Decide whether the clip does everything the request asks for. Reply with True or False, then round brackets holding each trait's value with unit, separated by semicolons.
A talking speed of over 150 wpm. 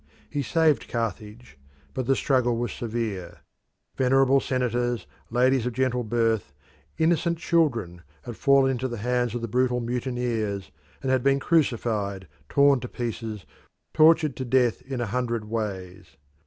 False (140 wpm)